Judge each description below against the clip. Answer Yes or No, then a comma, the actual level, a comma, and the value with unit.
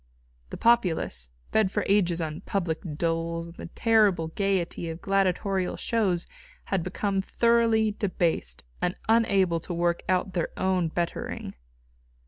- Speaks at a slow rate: Yes, slow, 130 wpm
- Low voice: No, medium, 185 Hz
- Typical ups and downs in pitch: Yes, average, 3.2 semitones